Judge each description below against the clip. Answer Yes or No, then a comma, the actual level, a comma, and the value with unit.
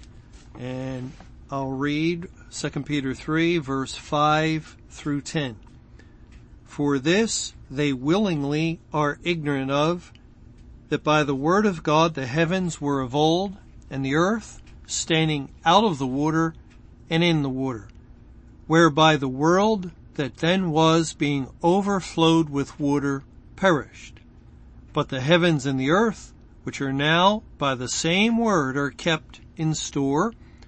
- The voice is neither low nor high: Yes, medium, 150 Hz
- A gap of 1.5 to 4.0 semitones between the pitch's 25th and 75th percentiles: Yes, average, 3.3 semitones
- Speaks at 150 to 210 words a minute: No, slow, 135 wpm